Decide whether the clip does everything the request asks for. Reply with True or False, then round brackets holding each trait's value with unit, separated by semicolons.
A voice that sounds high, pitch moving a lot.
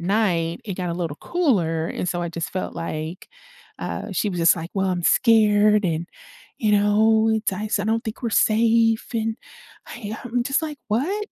False (210 Hz; 4.4 semitones)